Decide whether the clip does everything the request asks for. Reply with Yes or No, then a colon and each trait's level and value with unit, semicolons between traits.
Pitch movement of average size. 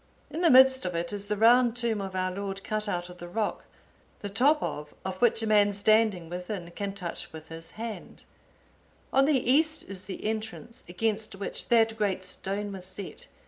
Yes: average, 3.5 semitones